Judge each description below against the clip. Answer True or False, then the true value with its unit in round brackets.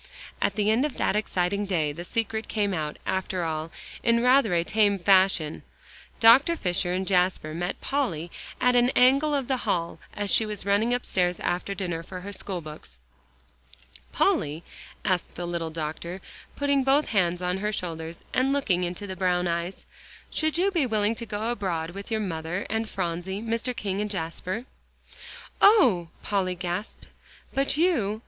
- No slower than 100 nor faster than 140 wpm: False (170 wpm)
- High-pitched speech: True (195 Hz)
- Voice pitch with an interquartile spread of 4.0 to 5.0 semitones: True (4.7 semitones)